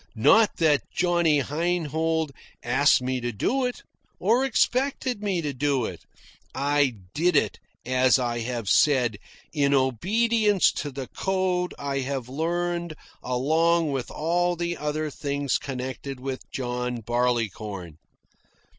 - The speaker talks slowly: Yes, slow, 130 wpm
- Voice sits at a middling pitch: Yes, medium, 145 Hz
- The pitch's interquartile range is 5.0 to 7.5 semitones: Yes, average, 5.3 semitones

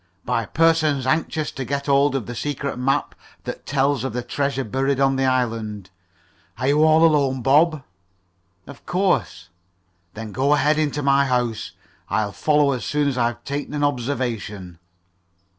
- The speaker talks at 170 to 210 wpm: No, average, 160 wpm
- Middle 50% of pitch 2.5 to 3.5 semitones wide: Yes, average, 3.0 semitones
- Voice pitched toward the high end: No, low, 135 Hz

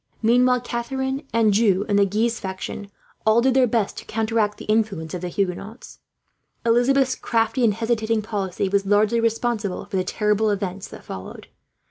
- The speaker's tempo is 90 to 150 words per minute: No, average, 160 wpm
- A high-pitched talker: Yes, high, 220 Hz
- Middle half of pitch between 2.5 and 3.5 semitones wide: Yes, average, 2.9 semitones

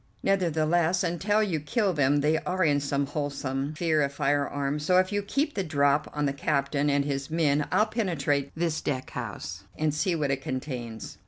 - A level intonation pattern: No, average, 3.7 semitones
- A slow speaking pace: No, average, 185 wpm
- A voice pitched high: No, medium, 150 Hz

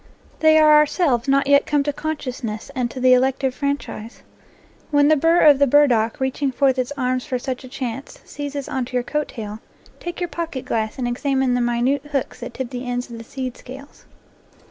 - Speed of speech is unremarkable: No, fast, 210 wpm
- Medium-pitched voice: No, very high, 265 Hz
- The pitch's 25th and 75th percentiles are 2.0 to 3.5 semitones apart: Yes, narrow, 2.6 semitones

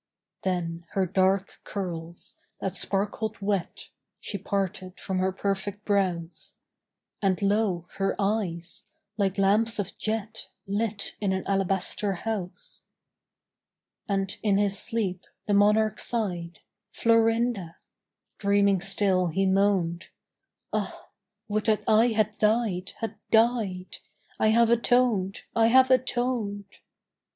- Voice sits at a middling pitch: No, high, 200 Hz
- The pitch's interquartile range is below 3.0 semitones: Yes, narrow, 2.6 semitones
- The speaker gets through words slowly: Yes, slow, 115 wpm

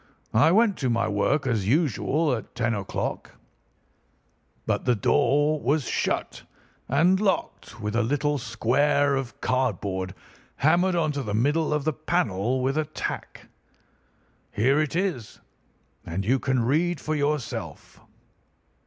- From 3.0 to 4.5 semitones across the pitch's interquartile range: No, average, 4.9 semitones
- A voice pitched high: No, low, 135 Hz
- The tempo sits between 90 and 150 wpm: Yes, slow, 135 wpm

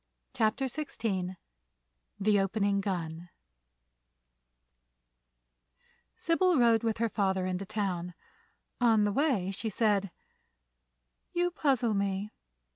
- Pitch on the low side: No, high, 210 Hz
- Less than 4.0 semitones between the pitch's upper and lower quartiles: Yes, average, 3.4 semitones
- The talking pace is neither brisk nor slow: No, slow, 95 wpm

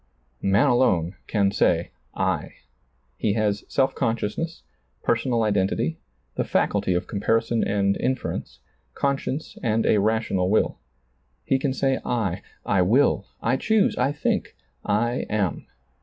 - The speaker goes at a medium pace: No, slow, 125 wpm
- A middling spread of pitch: Yes, average, 4.6 semitones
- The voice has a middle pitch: No, low, 110 Hz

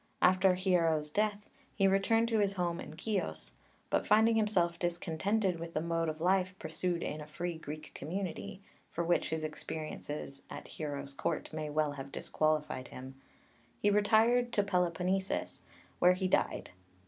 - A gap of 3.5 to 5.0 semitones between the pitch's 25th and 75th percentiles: Yes, average, 4.1 semitones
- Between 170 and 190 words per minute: No, average, 155 wpm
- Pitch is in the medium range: Yes, medium, 175 Hz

